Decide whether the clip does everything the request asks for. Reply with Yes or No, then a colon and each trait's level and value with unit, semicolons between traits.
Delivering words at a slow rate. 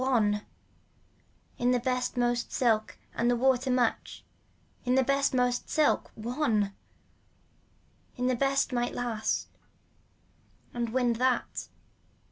Yes: slow, 110 wpm